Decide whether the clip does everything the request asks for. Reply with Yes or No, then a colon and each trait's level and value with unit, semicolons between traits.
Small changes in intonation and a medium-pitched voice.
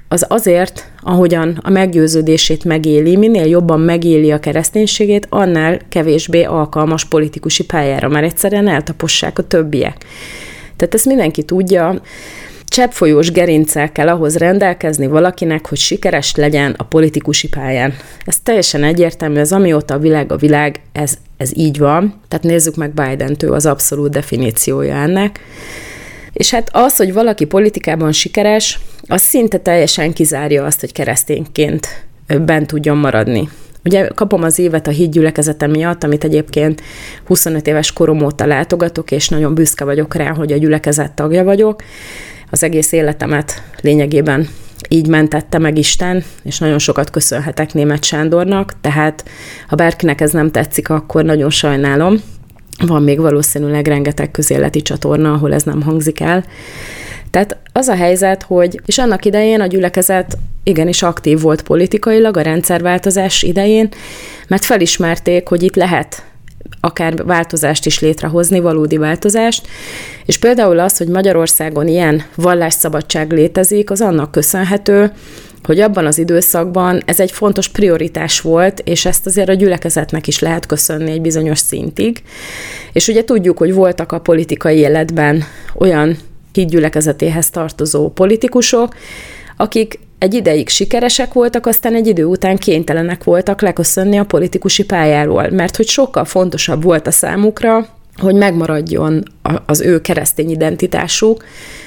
No: average, 3.6 semitones; medium, 160 Hz